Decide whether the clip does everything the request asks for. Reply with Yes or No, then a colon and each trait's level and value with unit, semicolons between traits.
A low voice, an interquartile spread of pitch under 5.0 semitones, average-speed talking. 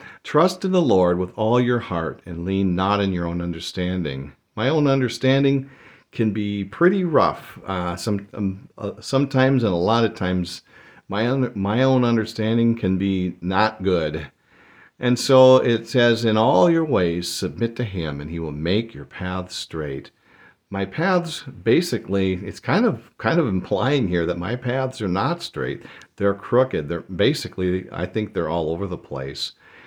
No: low, 105 Hz; wide, 5.4 semitones; average, 175 wpm